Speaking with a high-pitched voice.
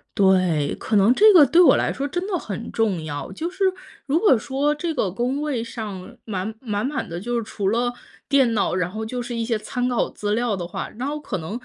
Yes: high, 230 Hz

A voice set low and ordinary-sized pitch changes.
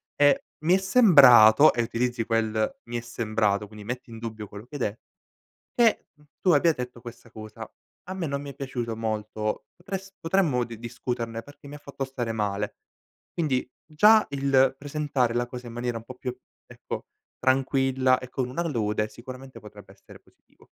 Yes: low, 125 Hz; average, 3.8 semitones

